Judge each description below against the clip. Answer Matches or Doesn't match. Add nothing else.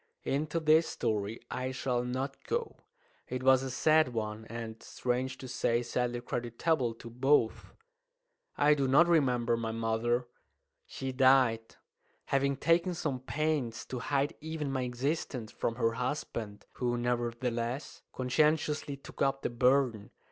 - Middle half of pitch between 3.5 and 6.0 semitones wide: Doesn't match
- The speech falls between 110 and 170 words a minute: Matches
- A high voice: Doesn't match